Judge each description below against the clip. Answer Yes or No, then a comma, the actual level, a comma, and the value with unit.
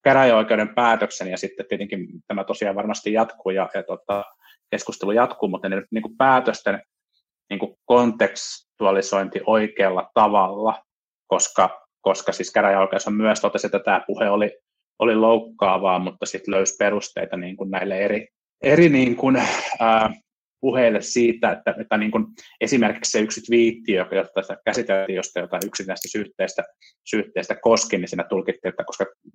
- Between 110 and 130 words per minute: No, average, 145 wpm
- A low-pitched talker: Yes, low, 110 Hz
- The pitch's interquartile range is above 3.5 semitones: No, average, 2.9 semitones